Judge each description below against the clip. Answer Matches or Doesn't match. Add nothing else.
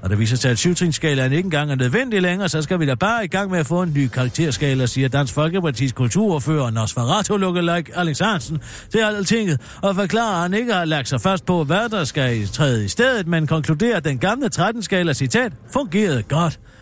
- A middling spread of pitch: Doesn't match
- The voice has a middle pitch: Matches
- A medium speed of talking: Matches